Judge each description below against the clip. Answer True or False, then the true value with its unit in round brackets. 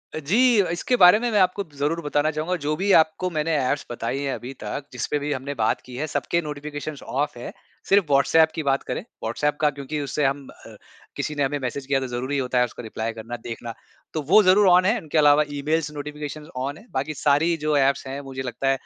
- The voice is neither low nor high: True (145 Hz)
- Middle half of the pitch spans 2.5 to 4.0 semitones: True (2.8 semitones)